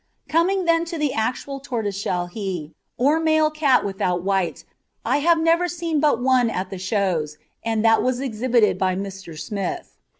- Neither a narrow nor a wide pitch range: No, wide, 8.1 semitones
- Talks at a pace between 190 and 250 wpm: No, average, 165 wpm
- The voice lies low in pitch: No, high, 235 Hz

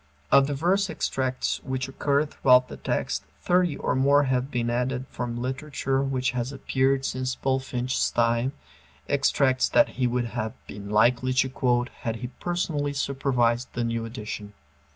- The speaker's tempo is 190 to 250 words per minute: No, average, 155 wpm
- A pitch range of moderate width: No, narrow, 2.2 semitones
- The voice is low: Yes, low, 130 Hz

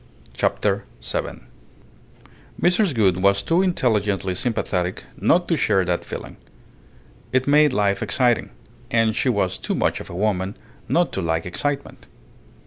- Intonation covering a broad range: Yes, wide, 6.9 semitones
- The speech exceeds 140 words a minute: No, slow, 135 wpm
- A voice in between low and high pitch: No, low, 105 Hz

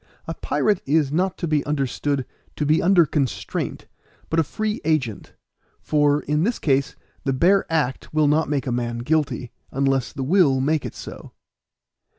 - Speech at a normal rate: Yes, average, 165 wpm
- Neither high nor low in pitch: Yes, medium, 150 Hz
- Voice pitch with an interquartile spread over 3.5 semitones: No, average, 3.1 semitones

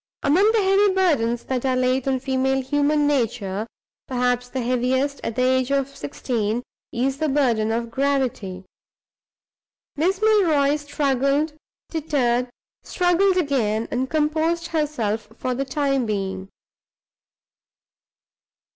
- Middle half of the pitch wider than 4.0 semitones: No, average, 3.7 semitones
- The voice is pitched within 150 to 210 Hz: No, very high, 265 Hz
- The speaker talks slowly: Yes, slow, 120 wpm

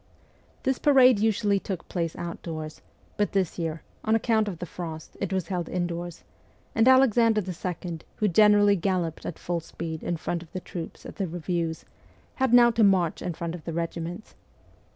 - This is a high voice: No, medium, 180 Hz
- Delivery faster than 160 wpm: Yes, average, 175 wpm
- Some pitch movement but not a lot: Yes, average, 3.9 semitones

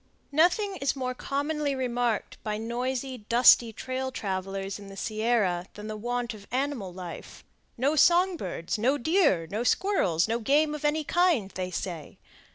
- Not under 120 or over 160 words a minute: Yes, average, 155 wpm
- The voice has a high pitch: Yes, high, 240 Hz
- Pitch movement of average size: No, wide, 6.1 semitones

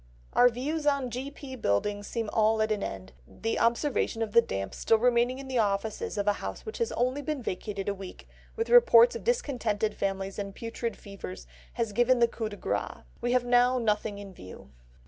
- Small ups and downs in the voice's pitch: No, average, 3.8 semitones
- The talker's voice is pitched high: Yes, high, 230 Hz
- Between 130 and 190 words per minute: No, average, 200 wpm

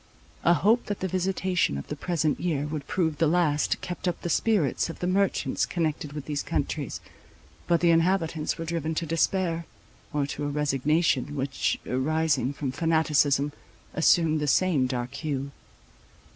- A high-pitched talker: No, medium, 160 Hz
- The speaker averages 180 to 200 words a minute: No, average, 160 wpm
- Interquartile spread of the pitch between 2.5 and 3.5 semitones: Yes, average, 3.1 semitones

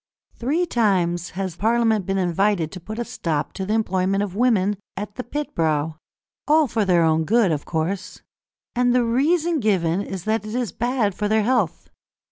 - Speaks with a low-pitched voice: No, high, 205 Hz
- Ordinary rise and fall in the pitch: Yes, average, 4.8 semitones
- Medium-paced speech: Yes, average, 180 wpm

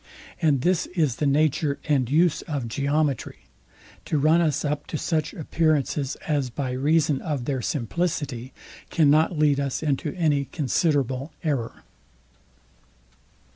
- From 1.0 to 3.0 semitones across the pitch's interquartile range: Yes, narrow, 2.4 semitones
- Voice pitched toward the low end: No, medium, 145 Hz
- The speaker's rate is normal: No, slow, 130 wpm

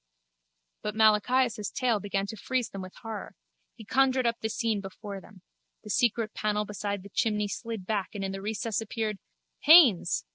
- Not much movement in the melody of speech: Yes, narrow, 2.3 semitones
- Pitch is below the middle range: No, high, 215 Hz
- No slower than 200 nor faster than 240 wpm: No, average, 175 wpm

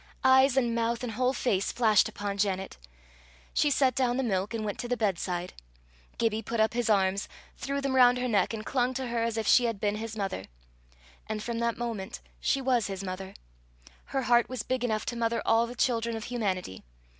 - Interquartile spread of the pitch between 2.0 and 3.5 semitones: Yes, average, 3.1 semitones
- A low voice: No, high, 230 Hz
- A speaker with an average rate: No, fast, 210 wpm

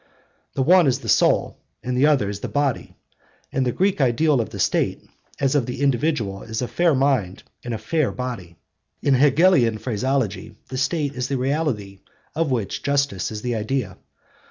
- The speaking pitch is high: No, low, 130 Hz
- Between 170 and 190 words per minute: Yes, average, 180 wpm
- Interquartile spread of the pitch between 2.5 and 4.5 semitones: Yes, average, 4.2 semitones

